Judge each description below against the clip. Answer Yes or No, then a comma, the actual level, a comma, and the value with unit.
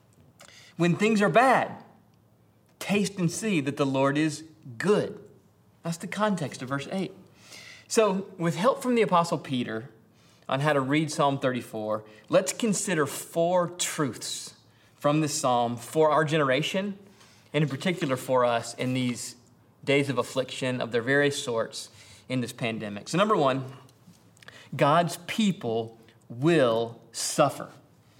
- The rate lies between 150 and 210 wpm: No, average, 140 wpm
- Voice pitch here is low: No, medium, 145 Hz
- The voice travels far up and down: Yes, wide, 5.7 semitones